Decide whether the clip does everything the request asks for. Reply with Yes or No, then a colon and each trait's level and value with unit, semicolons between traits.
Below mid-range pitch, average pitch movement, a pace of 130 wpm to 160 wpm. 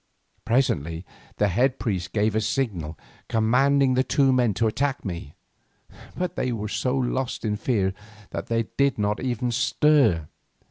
Yes: low, 115 Hz; average, 4.2 semitones; average, 150 wpm